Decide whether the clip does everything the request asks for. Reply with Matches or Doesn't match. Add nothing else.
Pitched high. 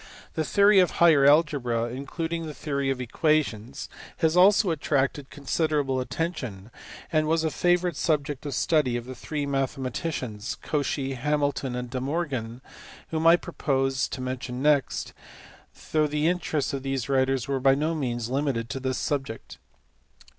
Doesn't match